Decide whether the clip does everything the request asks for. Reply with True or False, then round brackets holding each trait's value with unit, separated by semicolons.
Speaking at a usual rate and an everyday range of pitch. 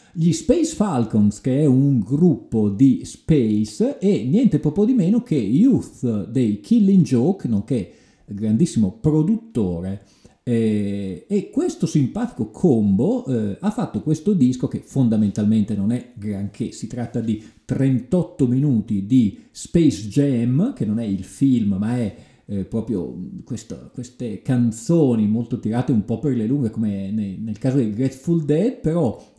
False (140 wpm; 7.5 semitones)